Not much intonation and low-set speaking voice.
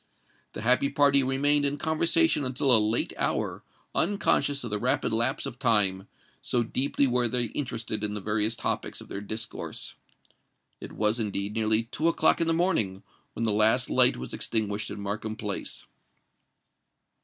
No: average, 4.6 semitones; low, 115 Hz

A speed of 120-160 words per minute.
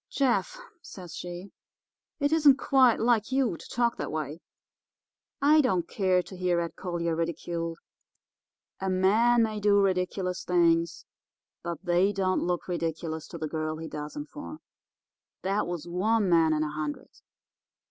Yes: average, 150 wpm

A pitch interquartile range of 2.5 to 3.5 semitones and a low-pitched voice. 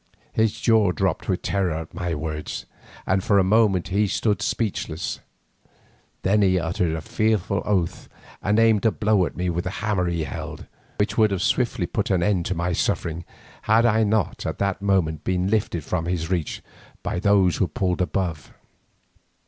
Yes: average, 3.2 semitones; very low, 95 Hz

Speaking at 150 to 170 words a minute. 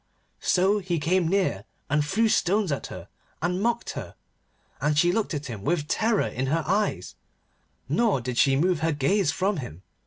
No: average, 180 wpm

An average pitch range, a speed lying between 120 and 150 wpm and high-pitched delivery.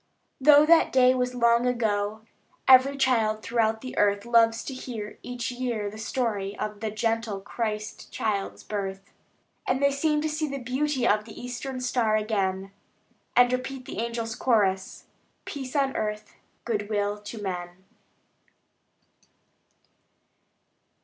Yes: average, 3.4 semitones; slow, 135 wpm; high, 230 Hz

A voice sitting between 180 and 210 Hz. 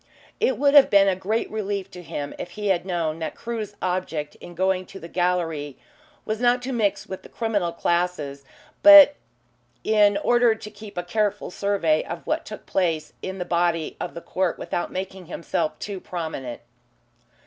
Yes: medium, 185 Hz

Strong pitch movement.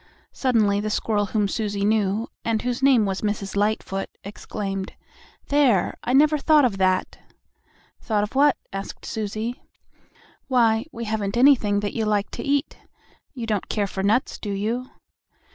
No: average, 3.4 semitones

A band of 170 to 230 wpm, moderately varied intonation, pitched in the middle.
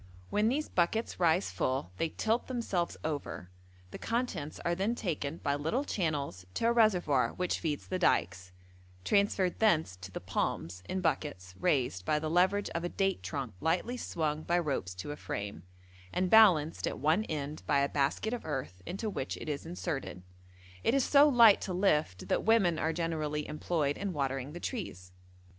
No: average, 180 wpm; wide, 5.8 semitones; medium, 160 Hz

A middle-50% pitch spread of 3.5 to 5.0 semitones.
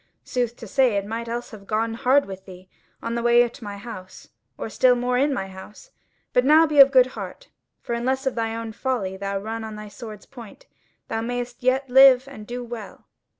No: average, 3.1 semitones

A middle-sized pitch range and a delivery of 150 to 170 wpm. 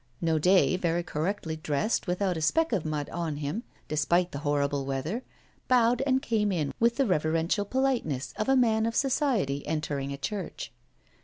No: wide, 7.0 semitones; average, 165 wpm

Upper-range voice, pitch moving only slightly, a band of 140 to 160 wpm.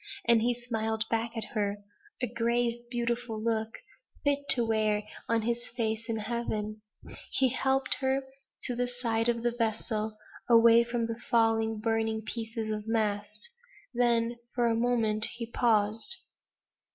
Yes: high, 230 Hz; narrow, 1.5 semitones; average, 145 wpm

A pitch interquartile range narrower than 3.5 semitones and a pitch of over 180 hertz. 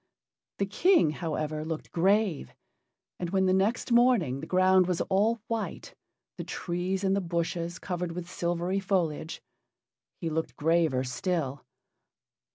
No: average, 3.0 semitones; medium, 175 Hz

